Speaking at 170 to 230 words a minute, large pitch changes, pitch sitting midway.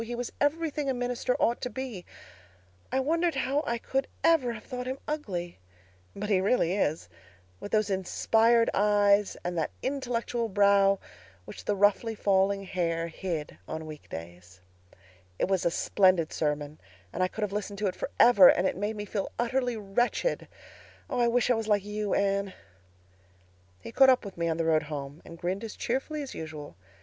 No: average, 180 wpm; wide, 6.2 semitones; high, 205 Hz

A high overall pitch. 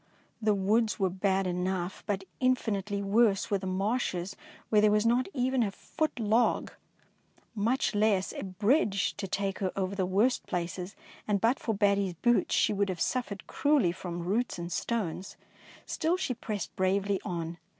Yes: high, 200 Hz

